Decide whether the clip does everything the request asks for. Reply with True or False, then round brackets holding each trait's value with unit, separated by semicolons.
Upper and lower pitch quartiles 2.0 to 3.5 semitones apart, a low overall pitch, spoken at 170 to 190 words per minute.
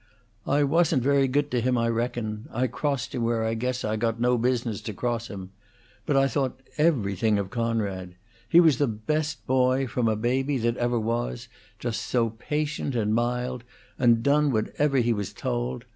True (3.1 semitones; 120 Hz; 185 wpm)